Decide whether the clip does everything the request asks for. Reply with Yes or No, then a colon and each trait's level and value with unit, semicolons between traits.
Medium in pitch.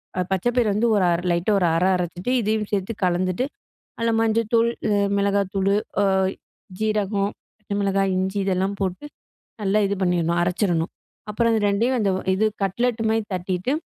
No: high, 200 Hz